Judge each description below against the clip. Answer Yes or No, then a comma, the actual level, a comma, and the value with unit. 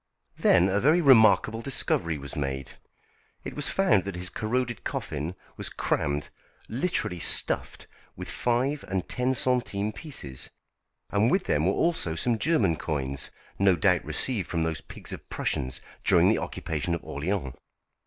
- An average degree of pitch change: No, wide, 7.8 semitones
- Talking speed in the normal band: Yes, average, 150 wpm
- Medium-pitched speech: No, very low, 95 Hz